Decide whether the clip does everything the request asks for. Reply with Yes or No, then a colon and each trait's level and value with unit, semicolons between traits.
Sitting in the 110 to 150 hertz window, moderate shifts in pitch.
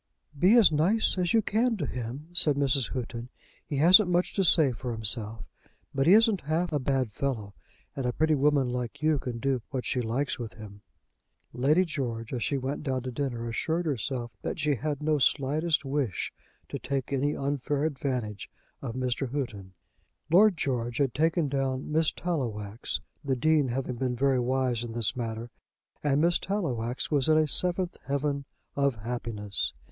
Yes: low, 135 Hz; average, 4.2 semitones